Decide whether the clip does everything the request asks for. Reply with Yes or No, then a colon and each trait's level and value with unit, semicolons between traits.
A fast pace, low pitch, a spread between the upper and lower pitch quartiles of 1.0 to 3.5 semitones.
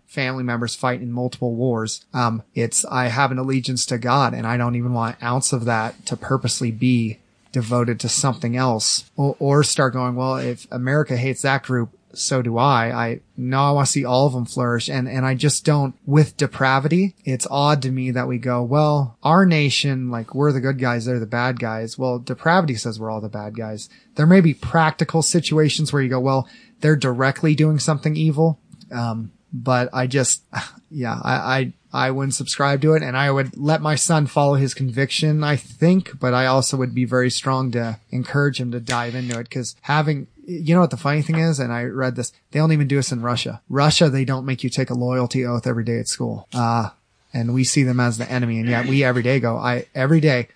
Yes: fast, 225 wpm; low, 130 Hz; average, 2.9 semitones